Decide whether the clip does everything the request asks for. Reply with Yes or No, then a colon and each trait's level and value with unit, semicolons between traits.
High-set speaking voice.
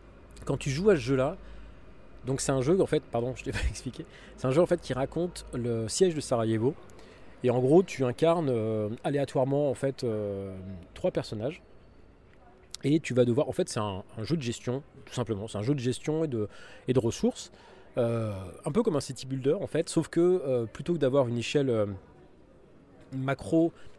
No: low, 130 Hz